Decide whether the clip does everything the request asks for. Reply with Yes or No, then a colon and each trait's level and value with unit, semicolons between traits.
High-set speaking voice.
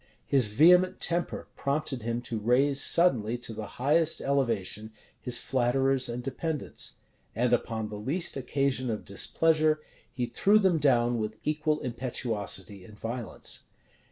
No: low, 125 Hz